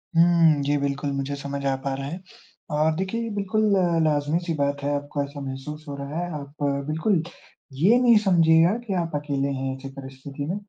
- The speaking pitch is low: No, medium, 145 Hz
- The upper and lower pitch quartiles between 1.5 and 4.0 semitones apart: Yes, average, 3.2 semitones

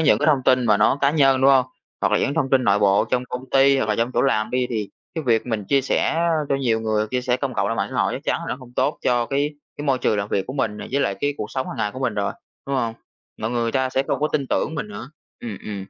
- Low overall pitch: Yes, low, 125 Hz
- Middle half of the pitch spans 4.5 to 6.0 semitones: No, average, 3.7 semitones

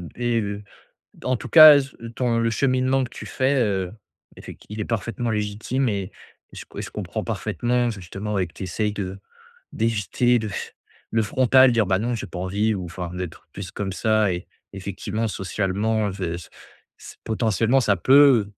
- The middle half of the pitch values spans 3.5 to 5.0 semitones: Yes, average, 3.8 semitones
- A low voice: Yes, low, 110 Hz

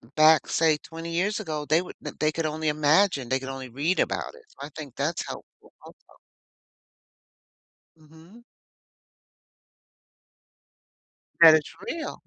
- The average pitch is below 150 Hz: No, medium, 155 Hz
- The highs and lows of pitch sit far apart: No, narrow, 2.2 semitones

